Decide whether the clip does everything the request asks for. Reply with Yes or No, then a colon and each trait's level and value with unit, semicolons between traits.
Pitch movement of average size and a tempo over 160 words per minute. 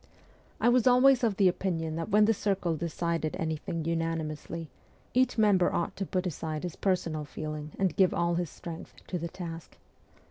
Yes: average, 3.2 semitones; average, 180 wpm